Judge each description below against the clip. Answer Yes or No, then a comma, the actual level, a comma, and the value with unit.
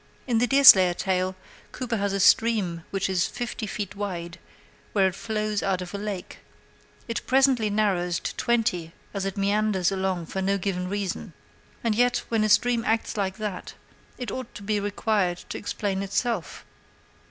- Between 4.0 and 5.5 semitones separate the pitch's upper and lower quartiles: No, average, 2.9 semitones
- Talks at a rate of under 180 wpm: Yes, average, 170 wpm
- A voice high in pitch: Yes, high, 200 Hz